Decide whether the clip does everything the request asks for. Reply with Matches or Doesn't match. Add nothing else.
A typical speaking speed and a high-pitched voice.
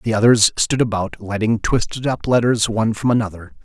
Doesn't match